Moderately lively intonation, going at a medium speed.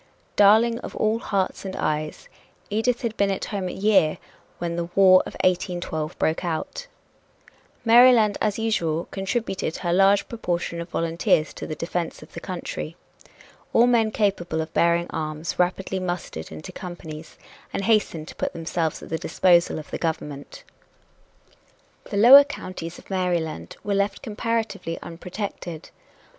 Yes: average, 4.1 semitones; average, 150 wpm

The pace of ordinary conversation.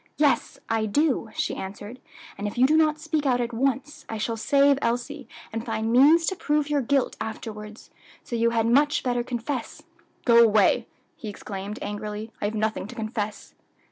Yes: average, 180 wpm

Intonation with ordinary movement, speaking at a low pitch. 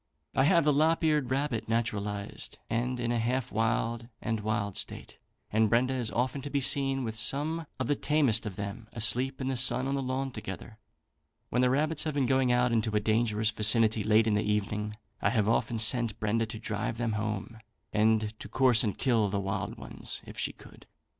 Yes: average, 3.4 semitones; low, 115 Hz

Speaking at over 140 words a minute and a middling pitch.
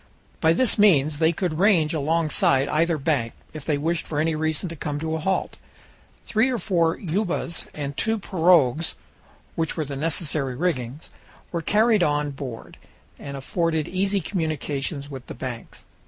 Yes: average, 155 wpm; medium, 160 Hz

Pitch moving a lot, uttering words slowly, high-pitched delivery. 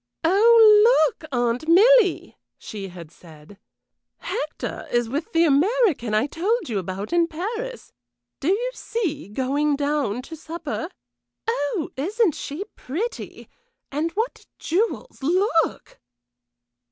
Yes: wide, 7.8 semitones; slow, 115 wpm; very high, 320 Hz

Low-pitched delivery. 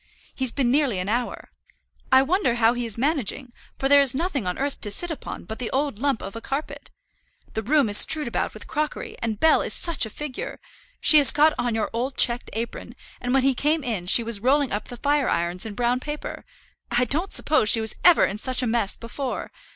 No: very high, 250 Hz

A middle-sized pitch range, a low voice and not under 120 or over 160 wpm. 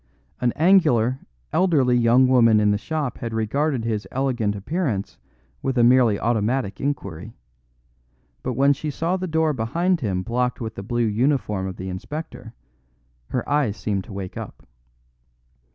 Yes: average, 4.9 semitones; low, 120 Hz; average, 150 wpm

